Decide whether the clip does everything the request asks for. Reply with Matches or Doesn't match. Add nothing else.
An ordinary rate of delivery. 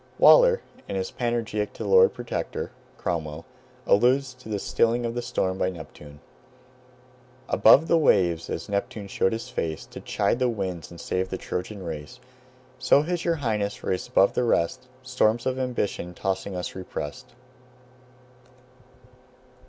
Matches